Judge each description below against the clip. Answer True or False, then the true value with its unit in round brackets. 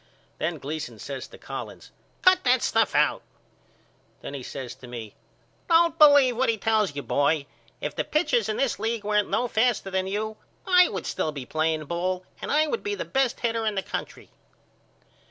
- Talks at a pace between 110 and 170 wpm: False (190 wpm)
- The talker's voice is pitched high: True (210 Hz)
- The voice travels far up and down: True (8.7 semitones)